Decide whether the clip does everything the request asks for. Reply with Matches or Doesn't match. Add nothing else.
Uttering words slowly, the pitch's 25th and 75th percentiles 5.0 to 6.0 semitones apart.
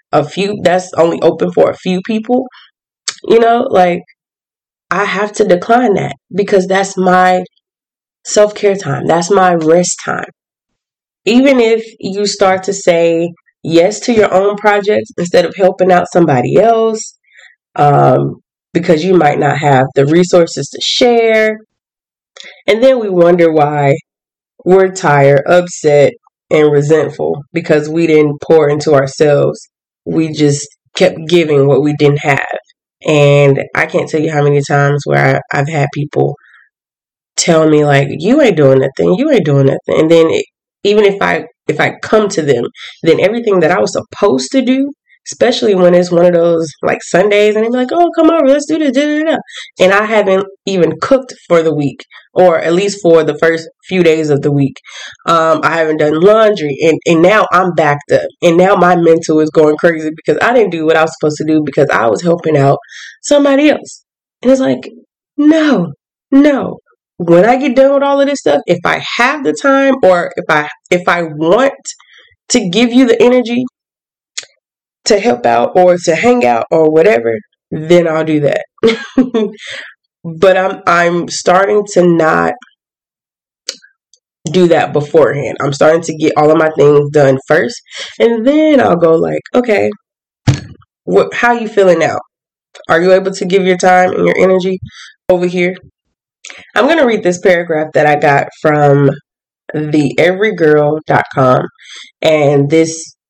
Doesn't match